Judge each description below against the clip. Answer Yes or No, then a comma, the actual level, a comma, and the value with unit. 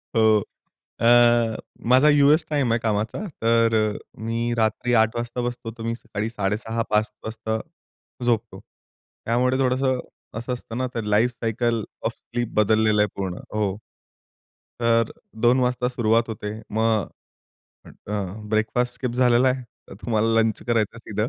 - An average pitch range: No, narrow, 1.9 semitones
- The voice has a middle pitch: No, low, 115 Hz